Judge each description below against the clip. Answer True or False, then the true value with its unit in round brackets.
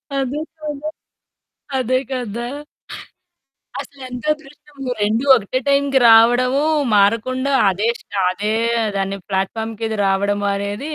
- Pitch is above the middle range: True (240 Hz)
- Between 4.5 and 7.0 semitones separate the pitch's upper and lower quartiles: True (5.0 semitones)